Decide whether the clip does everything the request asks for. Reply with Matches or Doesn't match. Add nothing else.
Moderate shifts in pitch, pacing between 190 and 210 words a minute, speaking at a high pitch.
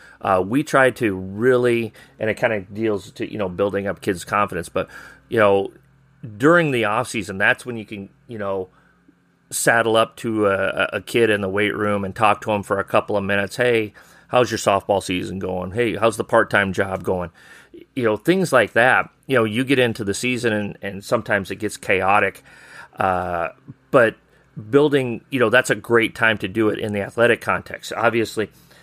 Doesn't match